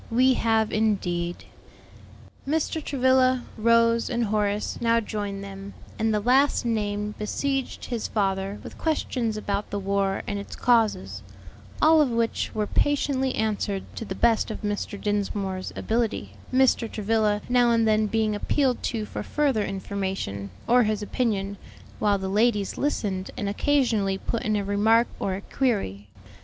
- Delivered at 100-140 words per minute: No, average, 150 wpm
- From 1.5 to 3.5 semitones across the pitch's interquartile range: Yes, average, 3.1 semitones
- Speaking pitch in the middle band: No, high, 215 Hz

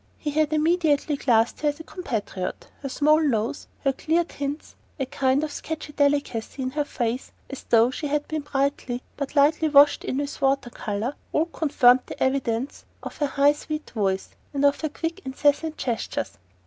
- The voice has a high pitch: Yes, very high, 285 Hz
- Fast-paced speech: No, average, 180 wpm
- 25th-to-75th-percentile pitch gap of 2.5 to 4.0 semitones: Yes, average, 2.8 semitones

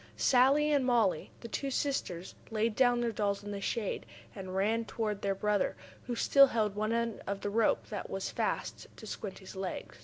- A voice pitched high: Yes, high, 215 Hz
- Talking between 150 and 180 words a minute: No, average, 195 wpm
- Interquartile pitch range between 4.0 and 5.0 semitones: No, average, 3.2 semitones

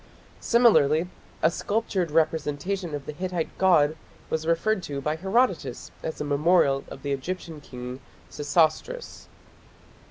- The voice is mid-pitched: Yes, medium, 160 Hz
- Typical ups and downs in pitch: Yes, average, 4.3 semitones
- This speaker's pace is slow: Yes, slow, 125 wpm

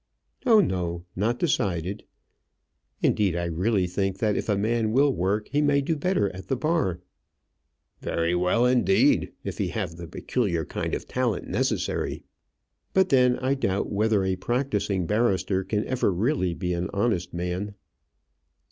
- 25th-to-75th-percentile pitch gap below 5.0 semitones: No, wide, 5.5 semitones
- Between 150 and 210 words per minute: Yes, average, 155 wpm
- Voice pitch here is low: Yes, low, 100 Hz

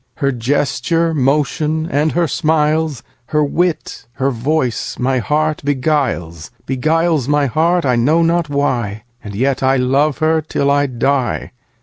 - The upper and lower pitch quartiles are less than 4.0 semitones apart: Yes, average, 3.5 semitones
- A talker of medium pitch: Yes, medium, 145 Hz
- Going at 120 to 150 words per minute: Yes, average, 145 wpm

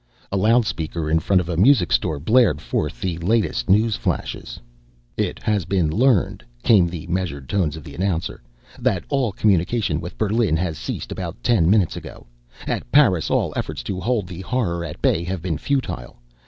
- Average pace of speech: Yes, average, 175 wpm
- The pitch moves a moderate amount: Yes, average, 5.0 semitones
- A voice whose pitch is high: No, very low, 90 Hz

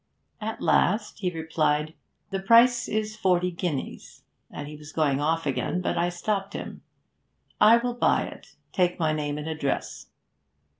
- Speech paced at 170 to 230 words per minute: No, average, 155 wpm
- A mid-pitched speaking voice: Yes, medium, 175 Hz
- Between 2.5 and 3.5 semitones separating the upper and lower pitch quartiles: No, wide, 5.5 semitones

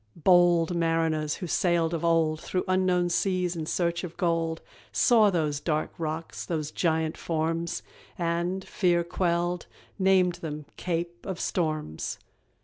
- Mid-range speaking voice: Yes, medium, 170 Hz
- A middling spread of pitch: No, narrow, 1.8 semitones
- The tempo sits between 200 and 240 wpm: No, slow, 135 wpm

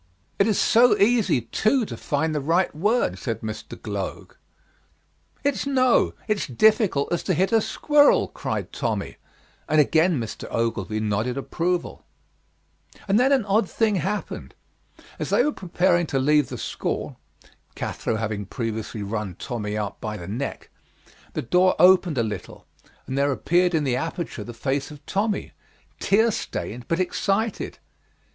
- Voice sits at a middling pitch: Yes, medium, 165 Hz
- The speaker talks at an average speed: Yes, average, 150 wpm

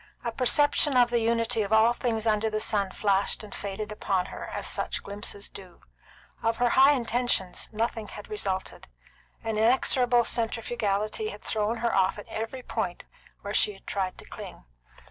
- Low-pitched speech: No, high, 220 Hz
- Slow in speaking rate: No, average, 165 wpm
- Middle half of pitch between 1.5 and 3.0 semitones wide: Yes, average, 2.7 semitones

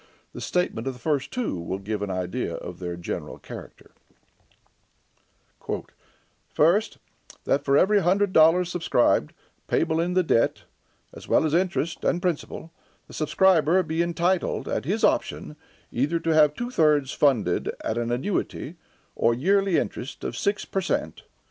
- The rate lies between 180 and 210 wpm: No, average, 150 wpm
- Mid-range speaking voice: Yes, medium, 155 Hz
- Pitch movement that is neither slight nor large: No, wide, 6.9 semitones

